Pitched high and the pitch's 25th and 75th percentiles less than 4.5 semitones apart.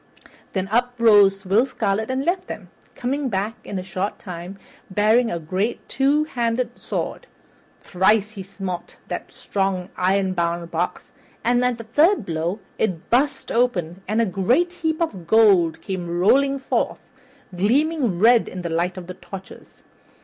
No: high, 205 Hz; average, 5.0 semitones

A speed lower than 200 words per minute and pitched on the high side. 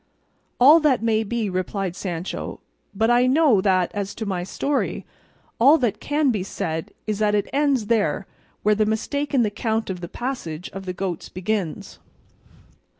Yes: average, 170 wpm; high, 215 Hz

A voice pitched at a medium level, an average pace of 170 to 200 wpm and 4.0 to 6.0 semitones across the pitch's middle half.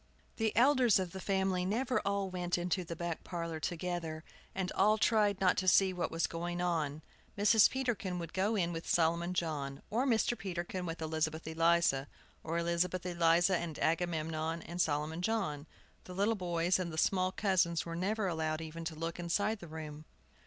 No: medium, 175 Hz; average, 180 wpm; average, 2.7 semitones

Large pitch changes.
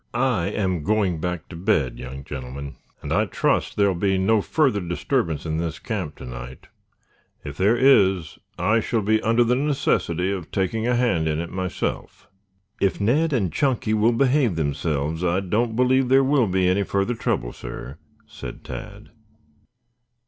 Yes: wide, 6.3 semitones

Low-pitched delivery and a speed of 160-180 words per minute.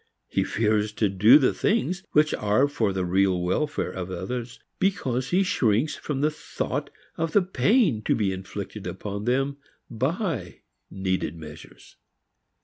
No: low, 115 Hz; average, 145 wpm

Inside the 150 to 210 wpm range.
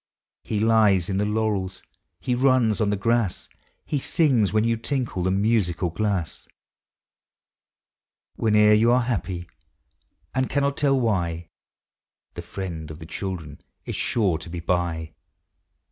No: slow, 135 wpm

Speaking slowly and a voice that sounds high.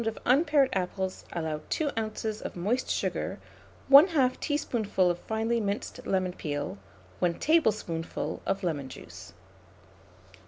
Yes: slow, 120 wpm; high, 205 Hz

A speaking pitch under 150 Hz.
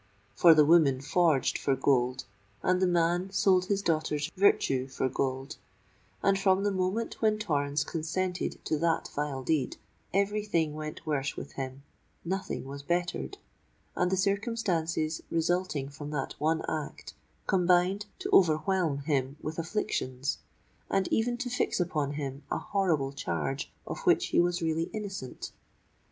No: medium, 165 Hz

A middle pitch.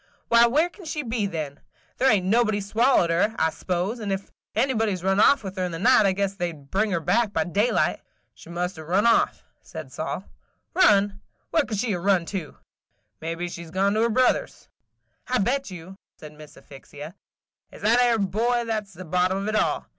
No: high, 200 Hz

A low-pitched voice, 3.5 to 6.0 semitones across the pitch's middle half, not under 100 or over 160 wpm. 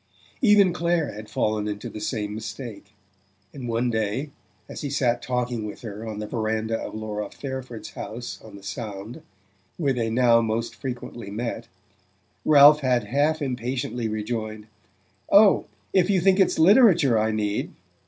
Yes: low, 120 Hz; average, 4.4 semitones; average, 155 wpm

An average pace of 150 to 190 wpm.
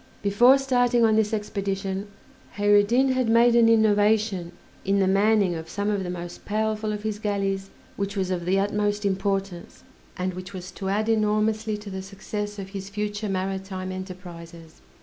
Yes: average, 175 wpm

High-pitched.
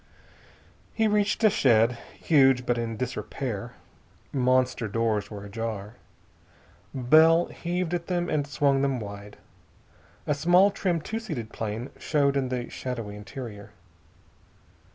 No: low, 130 Hz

